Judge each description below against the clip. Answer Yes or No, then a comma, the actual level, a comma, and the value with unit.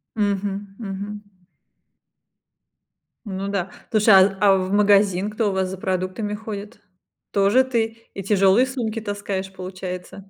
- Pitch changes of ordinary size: No, narrow, 1.8 semitones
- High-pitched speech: Yes, high, 200 Hz